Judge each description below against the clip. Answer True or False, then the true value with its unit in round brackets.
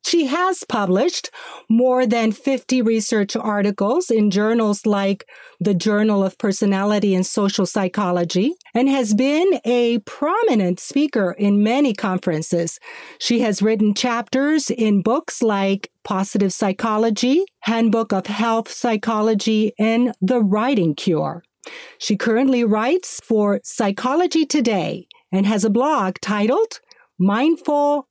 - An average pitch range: True (3.9 semitones)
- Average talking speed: False (120 wpm)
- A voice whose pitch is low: False (220 Hz)